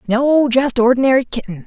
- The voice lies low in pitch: No, very high, 250 Hz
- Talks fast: No, average, 145 wpm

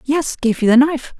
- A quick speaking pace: Yes, fast, 250 wpm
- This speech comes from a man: No, female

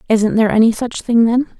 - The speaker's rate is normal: No, fast, 225 wpm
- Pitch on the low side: No, high, 230 Hz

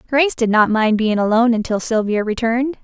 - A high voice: Yes, high, 230 Hz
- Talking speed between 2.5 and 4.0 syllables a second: No, 6.1 syllables/s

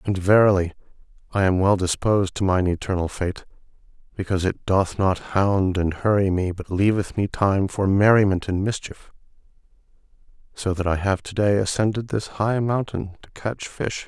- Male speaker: Yes, male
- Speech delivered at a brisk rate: No, average, 165 wpm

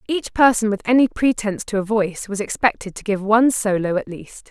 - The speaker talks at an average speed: No, fast, 215 wpm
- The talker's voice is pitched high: Yes, high, 215 Hz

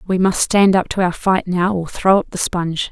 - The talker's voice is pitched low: No, medium, 185 Hz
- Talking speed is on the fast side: Yes, fast, 270 wpm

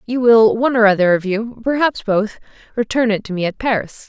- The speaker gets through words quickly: Yes, fast, 220 wpm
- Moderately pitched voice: No, high, 220 Hz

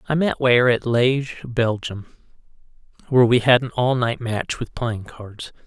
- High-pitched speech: No, low, 120 Hz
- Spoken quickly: No, average, 170 wpm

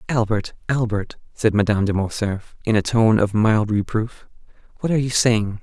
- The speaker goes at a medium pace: Yes, average, 170 wpm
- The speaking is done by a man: Yes, male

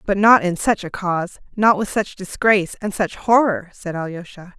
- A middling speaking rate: Yes, average, 195 wpm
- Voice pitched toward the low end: No, high, 195 Hz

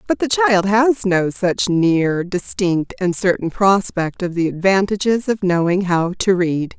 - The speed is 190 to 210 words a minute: No, average, 170 wpm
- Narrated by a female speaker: Yes, female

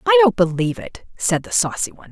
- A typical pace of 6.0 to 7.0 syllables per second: Yes, 6.6 syllables/s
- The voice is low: No, high, 225 Hz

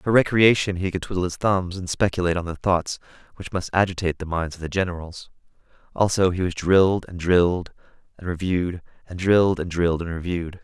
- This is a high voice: No, very low, 90 Hz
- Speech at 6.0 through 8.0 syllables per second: Yes, 6.1 syllables/s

